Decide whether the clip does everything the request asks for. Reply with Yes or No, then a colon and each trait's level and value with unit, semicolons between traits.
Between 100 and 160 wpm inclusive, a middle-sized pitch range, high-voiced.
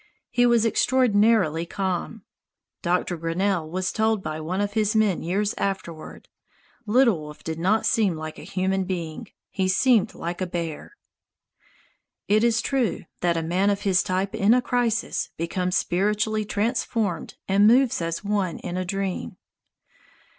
Yes: average, 150 wpm; average, 3.9 semitones; high, 195 Hz